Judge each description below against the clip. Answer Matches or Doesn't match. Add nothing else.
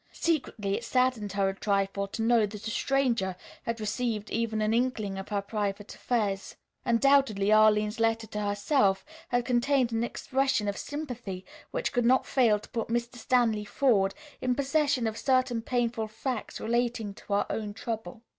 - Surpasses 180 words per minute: Doesn't match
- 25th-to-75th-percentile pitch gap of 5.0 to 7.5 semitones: Doesn't match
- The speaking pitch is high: Matches